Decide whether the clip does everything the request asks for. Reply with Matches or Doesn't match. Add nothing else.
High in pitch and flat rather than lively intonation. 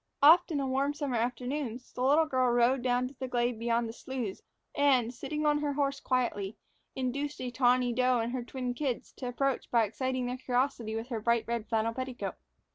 Matches